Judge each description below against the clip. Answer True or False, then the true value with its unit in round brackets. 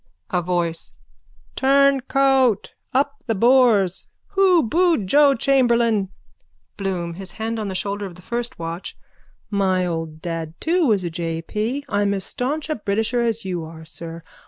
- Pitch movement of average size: False (6.9 semitones)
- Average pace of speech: True (155 wpm)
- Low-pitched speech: False (210 Hz)